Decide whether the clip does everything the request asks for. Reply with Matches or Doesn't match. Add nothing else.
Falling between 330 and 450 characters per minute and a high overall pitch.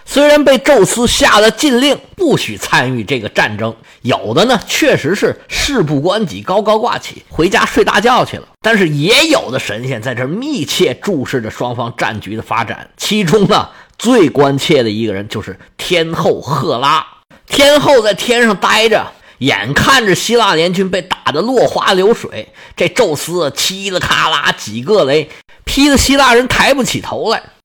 Doesn't match